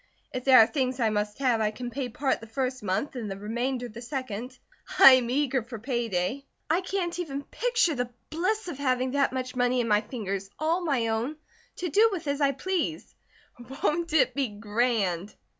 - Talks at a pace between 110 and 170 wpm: No, average, 200 wpm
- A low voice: No, very high, 255 Hz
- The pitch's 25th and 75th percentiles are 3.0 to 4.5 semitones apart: Yes, average, 4.0 semitones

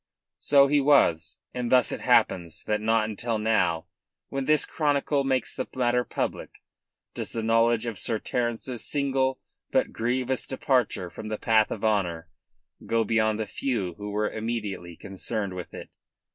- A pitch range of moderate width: Yes, average, 3.5 semitones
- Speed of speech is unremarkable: Yes, average, 160 wpm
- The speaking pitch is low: Yes, low, 115 Hz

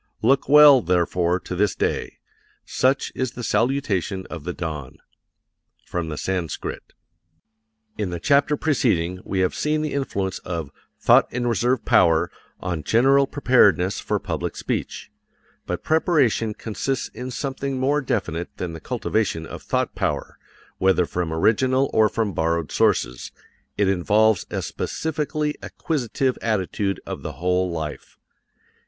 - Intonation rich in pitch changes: Yes, wide, 7.0 semitones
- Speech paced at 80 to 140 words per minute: Yes, slow, 135 wpm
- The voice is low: Yes, low, 105 Hz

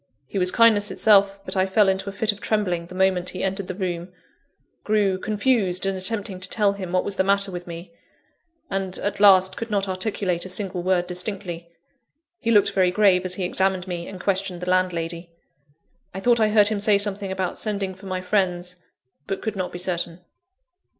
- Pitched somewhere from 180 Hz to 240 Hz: Yes, high, 190 Hz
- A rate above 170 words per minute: Yes, average, 200 wpm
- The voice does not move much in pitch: Yes, narrow, 2.0 semitones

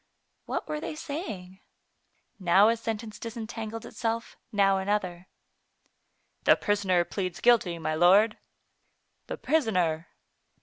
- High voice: Yes, high, 205 Hz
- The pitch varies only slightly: No, average, 3.8 semitones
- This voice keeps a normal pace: No, slow, 105 wpm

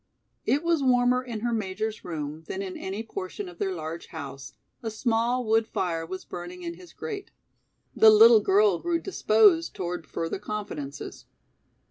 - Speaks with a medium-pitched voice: No, high, 205 Hz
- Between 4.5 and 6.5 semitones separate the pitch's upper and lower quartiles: Yes, average, 5.3 semitones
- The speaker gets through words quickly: No, average, 160 wpm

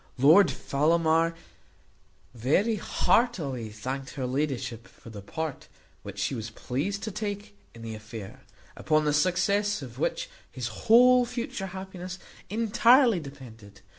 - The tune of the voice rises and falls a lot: Yes, wide, 8.7 semitones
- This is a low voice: No, medium, 155 Hz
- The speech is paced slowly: Yes, slow, 130 wpm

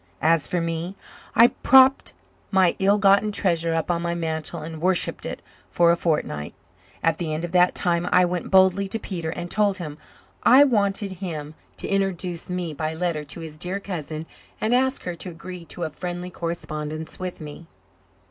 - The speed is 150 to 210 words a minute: Yes, average, 185 wpm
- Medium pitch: Yes, medium, 175 Hz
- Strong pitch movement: No, average, 2.8 semitones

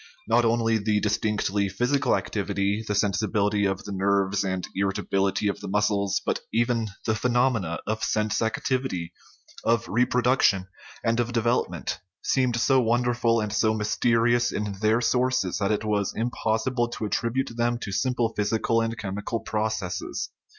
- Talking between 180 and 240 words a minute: No, average, 160 wpm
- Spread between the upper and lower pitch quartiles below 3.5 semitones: Yes, average, 2.8 semitones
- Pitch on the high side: No, low, 110 Hz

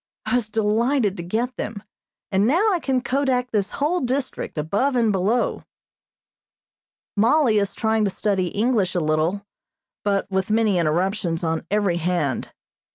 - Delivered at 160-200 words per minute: No, average, 150 wpm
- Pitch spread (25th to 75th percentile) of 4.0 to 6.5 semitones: Yes, average, 5.0 semitones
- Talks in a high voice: Yes, high, 210 Hz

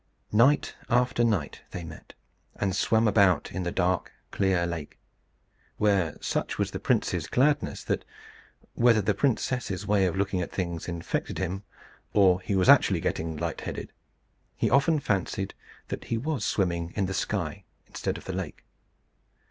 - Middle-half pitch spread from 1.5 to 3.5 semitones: No, average, 4.2 semitones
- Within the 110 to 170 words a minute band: Yes, average, 155 wpm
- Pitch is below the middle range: Yes, very low, 95 Hz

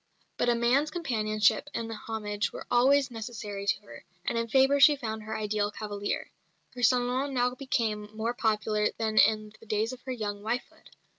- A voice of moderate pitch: No, high, 225 Hz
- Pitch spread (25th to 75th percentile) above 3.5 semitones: No, average, 2.8 semitones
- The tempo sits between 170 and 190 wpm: Yes, average, 180 wpm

